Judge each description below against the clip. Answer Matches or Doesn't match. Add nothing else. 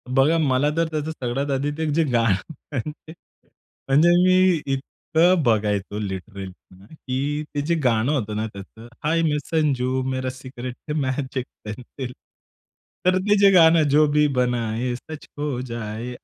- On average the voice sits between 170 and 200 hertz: Doesn't match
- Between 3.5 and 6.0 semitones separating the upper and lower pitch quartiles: Matches